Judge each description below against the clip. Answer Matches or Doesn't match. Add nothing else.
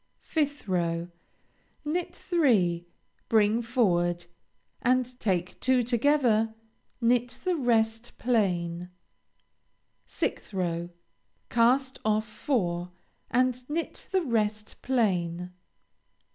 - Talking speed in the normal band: Doesn't match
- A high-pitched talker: Matches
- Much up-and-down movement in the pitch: Matches